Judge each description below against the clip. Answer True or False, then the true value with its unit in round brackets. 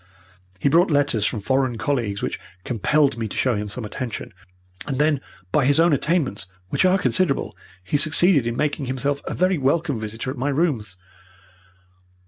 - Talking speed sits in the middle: True (170 wpm)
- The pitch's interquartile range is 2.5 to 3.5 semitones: False (4.6 semitones)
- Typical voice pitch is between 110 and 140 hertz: True (135 Hz)